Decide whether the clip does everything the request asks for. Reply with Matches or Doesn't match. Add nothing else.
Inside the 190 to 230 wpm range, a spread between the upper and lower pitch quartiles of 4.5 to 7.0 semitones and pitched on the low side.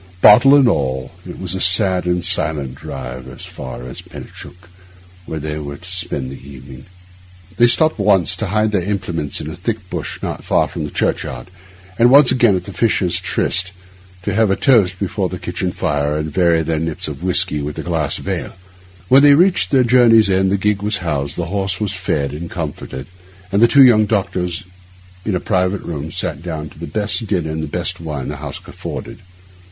Matches